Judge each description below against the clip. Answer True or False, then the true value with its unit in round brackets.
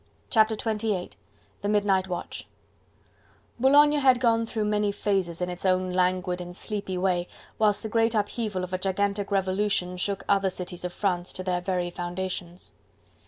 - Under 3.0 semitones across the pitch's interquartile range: True (2.6 semitones)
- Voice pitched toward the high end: True (195 Hz)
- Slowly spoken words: False (160 wpm)